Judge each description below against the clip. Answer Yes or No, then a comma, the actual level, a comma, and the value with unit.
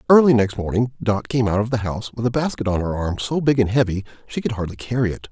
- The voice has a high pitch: No, low, 110 Hz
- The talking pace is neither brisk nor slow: No, fast, 270 wpm